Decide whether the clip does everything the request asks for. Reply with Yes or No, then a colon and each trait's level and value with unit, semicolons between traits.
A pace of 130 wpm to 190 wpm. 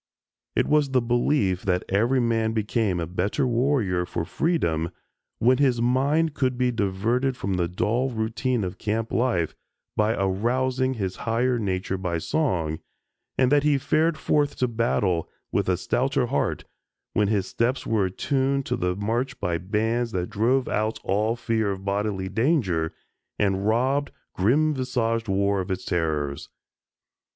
Yes: average, 155 wpm